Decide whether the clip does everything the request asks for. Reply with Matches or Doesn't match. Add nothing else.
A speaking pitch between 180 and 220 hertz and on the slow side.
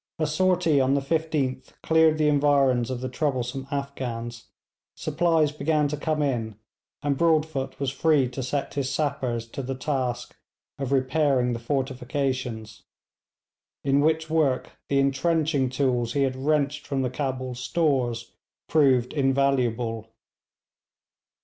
Doesn't match